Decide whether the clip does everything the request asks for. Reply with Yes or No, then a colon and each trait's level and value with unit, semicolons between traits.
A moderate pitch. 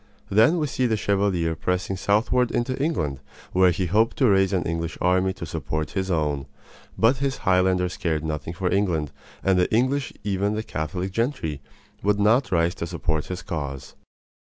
No: very low, 95 Hz